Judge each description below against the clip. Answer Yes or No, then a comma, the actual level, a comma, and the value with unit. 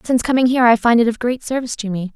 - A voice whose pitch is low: No, high, 235 Hz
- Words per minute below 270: No, fast, 305 wpm